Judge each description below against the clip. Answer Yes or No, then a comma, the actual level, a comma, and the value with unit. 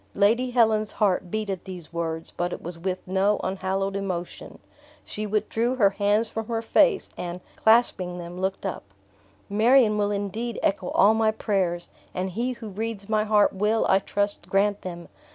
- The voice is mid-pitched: No, high, 205 Hz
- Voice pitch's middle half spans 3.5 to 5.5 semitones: No, average, 2.8 semitones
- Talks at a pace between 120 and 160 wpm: No, average, 170 wpm